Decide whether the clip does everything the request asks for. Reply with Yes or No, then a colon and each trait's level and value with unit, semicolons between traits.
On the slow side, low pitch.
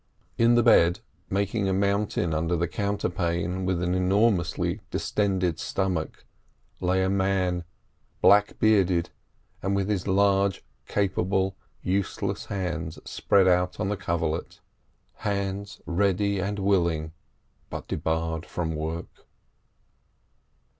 Yes: slow, 110 wpm; very low, 95 Hz